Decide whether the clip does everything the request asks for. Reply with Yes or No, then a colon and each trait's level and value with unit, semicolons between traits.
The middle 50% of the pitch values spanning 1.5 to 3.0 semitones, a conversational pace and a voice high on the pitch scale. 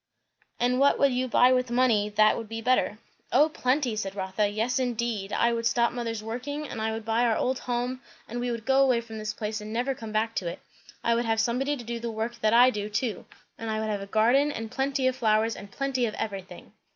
No: average, 2.7 semitones; fast, 245 wpm; high, 235 Hz